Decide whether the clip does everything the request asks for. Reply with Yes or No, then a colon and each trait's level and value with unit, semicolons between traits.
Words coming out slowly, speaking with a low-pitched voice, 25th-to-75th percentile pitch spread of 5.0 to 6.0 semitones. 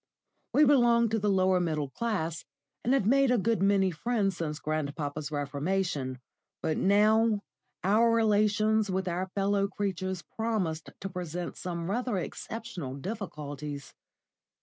No: slow, 130 wpm; high, 195 Hz; wide, 5.4 semitones